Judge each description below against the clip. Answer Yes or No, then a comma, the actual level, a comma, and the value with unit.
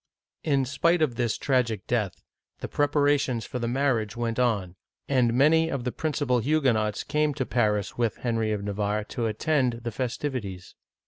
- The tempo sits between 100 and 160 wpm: No, average, 170 wpm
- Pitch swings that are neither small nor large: Yes, average, 4.4 semitones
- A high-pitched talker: No, low, 120 Hz